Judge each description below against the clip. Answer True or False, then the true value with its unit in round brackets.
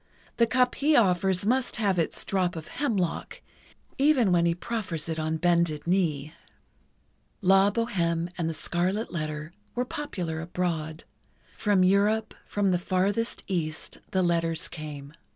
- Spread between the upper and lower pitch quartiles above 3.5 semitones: True (3.9 semitones)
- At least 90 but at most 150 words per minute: True (140 wpm)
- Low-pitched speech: False (180 Hz)